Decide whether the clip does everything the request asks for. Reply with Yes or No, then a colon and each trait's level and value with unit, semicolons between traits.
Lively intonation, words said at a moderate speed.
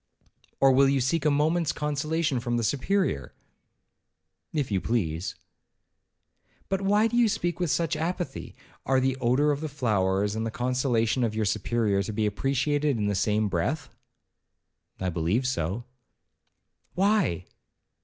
Yes: wide, 6.2 semitones; average, 145 wpm